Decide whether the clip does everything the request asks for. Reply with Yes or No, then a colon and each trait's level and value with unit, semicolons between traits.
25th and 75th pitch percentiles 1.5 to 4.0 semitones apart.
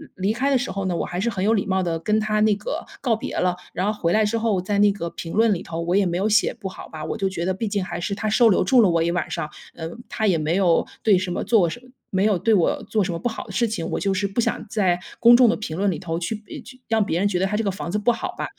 Yes: average, 3.5 semitones